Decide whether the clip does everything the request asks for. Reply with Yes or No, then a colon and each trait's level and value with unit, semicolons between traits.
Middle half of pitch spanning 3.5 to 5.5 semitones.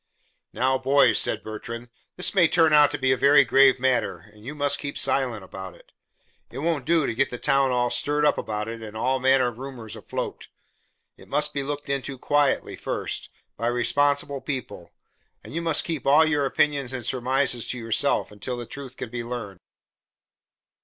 No: average, 3.1 semitones